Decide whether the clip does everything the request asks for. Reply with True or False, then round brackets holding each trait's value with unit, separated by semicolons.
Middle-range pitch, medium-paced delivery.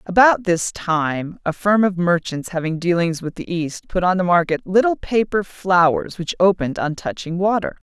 True (180 Hz; 180 wpm)